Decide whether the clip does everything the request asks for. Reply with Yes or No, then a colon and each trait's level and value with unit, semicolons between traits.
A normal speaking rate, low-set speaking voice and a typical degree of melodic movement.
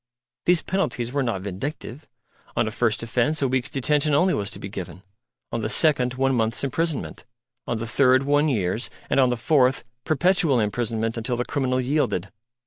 Yes: average, 180 wpm; low, 130 Hz; average, 4.1 semitones